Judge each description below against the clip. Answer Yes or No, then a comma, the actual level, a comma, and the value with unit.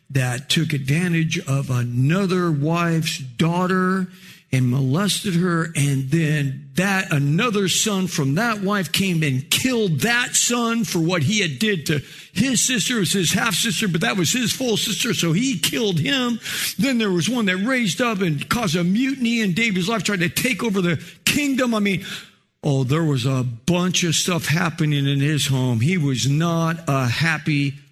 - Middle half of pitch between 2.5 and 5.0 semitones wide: No, wide, 5.6 semitones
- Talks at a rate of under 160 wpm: No, average, 180 wpm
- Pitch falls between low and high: Yes, medium, 175 Hz